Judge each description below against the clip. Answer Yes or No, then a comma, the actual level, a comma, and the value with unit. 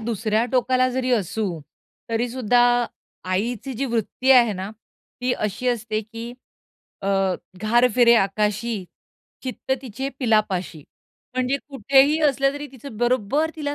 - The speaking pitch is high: Yes, high, 235 Hz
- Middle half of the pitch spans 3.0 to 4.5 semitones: Yes, average, 3.3 semitones